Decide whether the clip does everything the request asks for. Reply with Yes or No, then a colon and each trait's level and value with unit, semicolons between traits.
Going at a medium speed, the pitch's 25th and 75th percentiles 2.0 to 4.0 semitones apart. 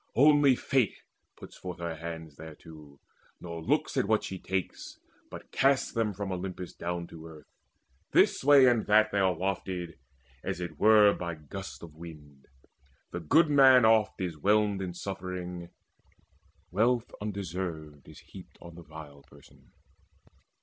No: average, 150 wpm; average, 4.5 semitones